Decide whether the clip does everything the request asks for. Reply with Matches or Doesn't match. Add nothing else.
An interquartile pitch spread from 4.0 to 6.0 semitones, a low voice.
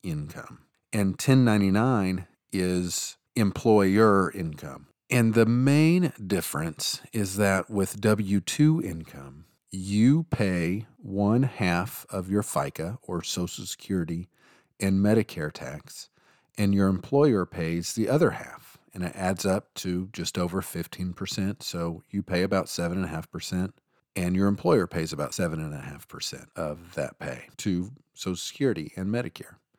Doesn't match